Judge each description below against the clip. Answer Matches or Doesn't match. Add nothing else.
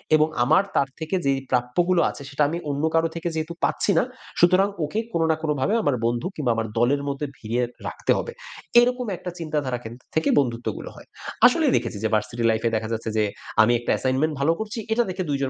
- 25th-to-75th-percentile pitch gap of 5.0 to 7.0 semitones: Matches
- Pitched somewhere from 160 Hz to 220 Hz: Doesn't match